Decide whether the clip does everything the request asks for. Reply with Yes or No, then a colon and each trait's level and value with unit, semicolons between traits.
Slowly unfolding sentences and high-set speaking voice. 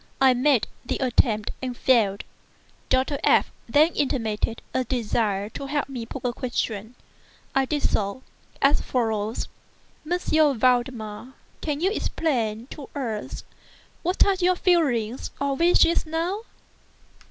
Yes: slow, 130 wpm; very high, 260 Hz